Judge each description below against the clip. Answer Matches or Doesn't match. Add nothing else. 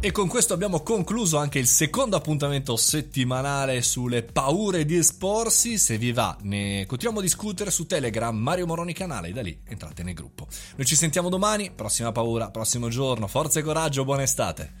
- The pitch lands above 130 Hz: Matches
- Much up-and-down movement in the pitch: Matches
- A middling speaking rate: Doesn't match